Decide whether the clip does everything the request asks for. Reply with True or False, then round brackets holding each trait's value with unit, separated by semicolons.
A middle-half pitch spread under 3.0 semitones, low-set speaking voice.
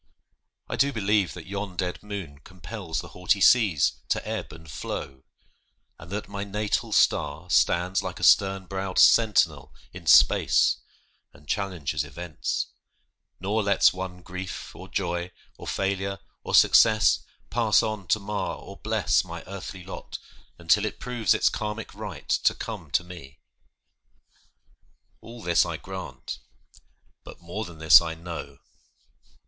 False (3.3 semitones; 95 Hz)